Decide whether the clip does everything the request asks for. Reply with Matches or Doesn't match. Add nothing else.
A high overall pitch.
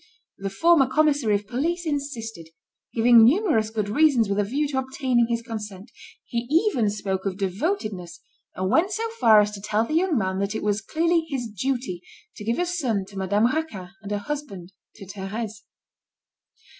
Matches